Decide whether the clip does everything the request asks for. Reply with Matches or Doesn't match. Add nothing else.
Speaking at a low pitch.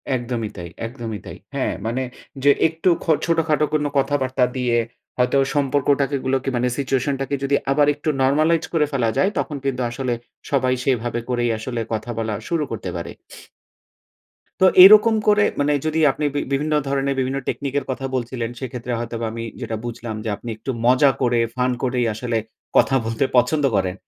Matches